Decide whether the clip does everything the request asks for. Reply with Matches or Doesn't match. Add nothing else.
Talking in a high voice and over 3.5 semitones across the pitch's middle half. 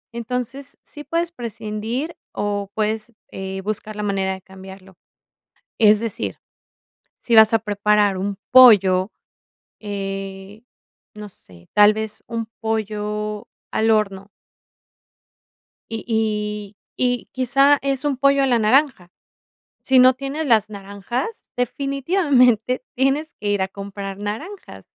Matches